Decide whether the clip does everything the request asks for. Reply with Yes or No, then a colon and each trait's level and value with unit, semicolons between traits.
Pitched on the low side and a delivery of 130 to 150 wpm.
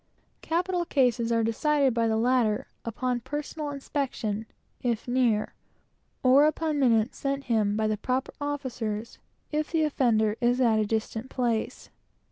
No: very high, 250 Hz; average, 140 wpm